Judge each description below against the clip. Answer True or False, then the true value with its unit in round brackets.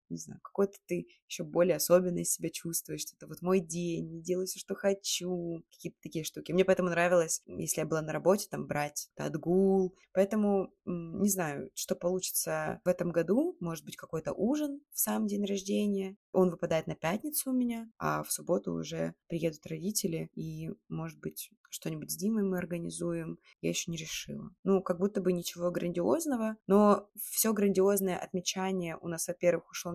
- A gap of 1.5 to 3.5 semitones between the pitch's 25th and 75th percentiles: True (3.1 semitones)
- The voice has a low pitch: False (180 Hz)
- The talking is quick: True (170 wpm)